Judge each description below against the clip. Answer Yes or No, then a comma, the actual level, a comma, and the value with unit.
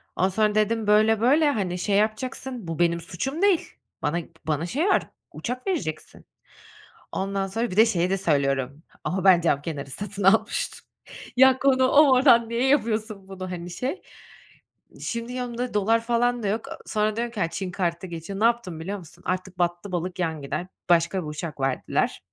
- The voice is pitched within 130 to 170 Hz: No, high, 200 Hz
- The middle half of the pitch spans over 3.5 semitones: Yes, average, 5.2 semitones